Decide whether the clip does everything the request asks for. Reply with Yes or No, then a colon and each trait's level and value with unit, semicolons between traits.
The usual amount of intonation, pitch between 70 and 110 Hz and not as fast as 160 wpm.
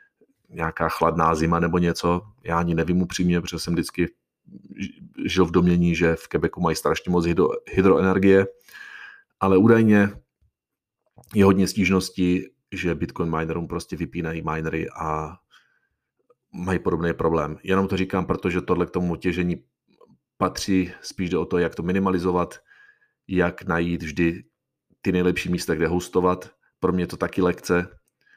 No: narrow, 2.1 semitones; very low, 90 Hz; average, 140 wpm